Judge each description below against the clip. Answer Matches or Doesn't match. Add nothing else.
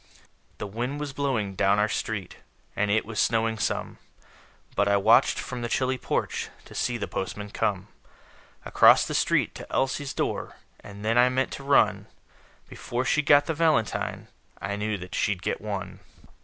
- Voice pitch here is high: Doesn't match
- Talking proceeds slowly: Doesn't match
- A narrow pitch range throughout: Doesn't match